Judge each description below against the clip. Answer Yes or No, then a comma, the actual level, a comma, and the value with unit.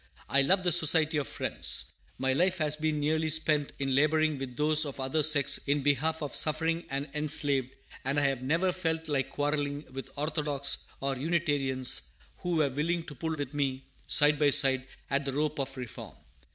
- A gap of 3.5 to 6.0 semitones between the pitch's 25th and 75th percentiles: No, narrow, 2.4 semitones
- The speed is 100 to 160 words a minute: No, average, 190 wpm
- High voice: No, medium, 145 Hz